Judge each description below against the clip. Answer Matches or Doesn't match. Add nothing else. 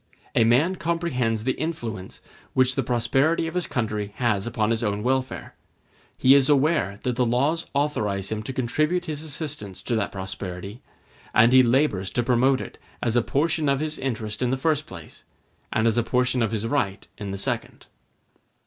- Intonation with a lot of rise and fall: Doesn't match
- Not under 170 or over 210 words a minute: Matches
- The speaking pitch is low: Matches